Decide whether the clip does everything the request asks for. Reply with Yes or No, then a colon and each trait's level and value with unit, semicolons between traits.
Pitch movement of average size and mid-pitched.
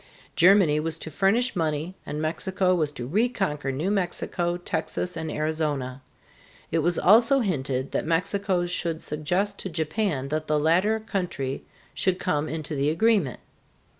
Yes: average, 4.1 semitones; medium, 165 Hz